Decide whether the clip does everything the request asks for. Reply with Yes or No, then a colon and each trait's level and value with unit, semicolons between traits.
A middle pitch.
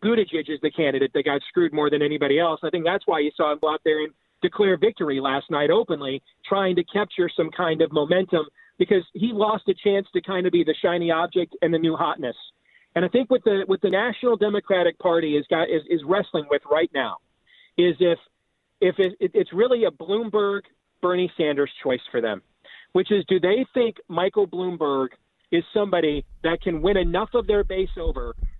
Yes: medium, 175 Hz